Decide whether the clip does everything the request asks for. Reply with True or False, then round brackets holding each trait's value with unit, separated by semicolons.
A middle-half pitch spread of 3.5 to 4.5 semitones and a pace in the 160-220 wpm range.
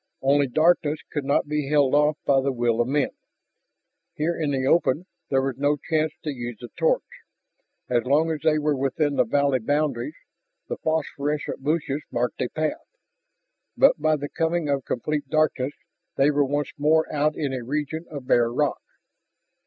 False (2.4 semitones; 175 wpm)